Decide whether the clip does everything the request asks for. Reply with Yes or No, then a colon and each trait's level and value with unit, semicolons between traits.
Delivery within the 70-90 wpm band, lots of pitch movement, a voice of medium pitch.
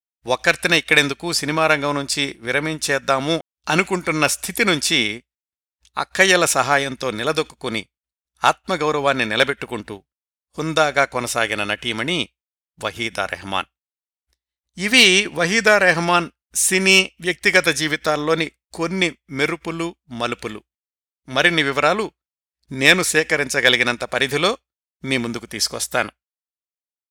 Yes: average, 75 wpm; wide, 6.0 semitones; medium, 145 Hz